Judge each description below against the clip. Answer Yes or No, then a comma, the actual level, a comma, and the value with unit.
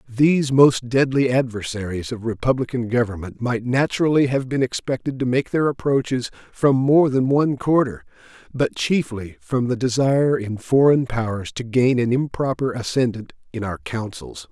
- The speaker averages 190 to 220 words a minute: No, average, 155 wpm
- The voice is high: No, low, 125 Hz